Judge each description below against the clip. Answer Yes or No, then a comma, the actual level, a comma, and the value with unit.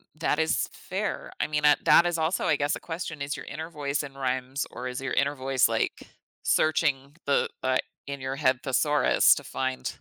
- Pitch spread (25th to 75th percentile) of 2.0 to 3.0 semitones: Yes, narrow, 2.6 semitones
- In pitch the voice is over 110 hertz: Yes, medium, 140 Hz